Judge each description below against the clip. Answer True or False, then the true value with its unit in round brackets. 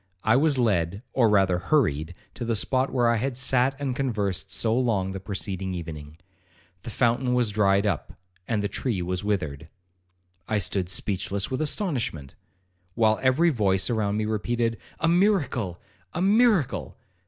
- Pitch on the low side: True (110 Hz)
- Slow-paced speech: False (155 wpm)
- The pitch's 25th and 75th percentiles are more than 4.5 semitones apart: True (5.1 semitones)